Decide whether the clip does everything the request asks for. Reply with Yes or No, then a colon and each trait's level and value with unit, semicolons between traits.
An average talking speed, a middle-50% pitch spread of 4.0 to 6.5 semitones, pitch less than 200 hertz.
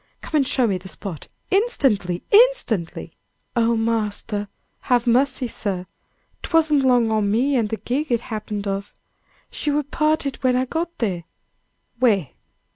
No: average, 145 wpm; wide, 5.4 semitones; high, 235 Hz